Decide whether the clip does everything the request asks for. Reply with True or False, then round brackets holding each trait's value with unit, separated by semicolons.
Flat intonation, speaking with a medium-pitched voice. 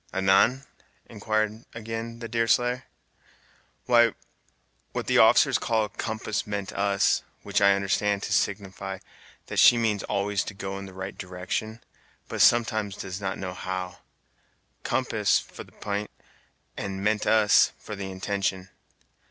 False (2.3 semitones; 100 Hz)